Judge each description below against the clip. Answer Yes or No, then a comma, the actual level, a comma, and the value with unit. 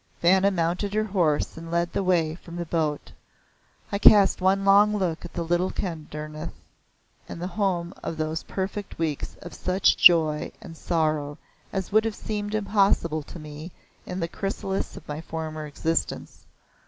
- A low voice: No, medium, 170 Hz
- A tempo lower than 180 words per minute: Yes, average, 160 wpm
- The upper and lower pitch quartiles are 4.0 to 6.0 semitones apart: No, average, 3.6 semitones